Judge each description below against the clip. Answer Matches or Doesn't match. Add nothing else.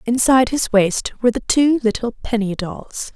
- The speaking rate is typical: Matches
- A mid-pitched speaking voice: Doesn't match